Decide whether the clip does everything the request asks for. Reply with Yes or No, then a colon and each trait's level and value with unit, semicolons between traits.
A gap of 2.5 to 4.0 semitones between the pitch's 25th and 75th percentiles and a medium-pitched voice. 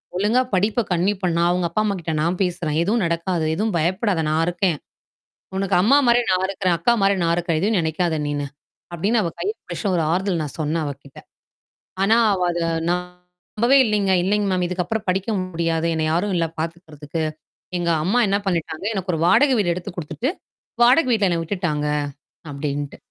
Yes: average, 3.3 semitones; medium, 180 Hz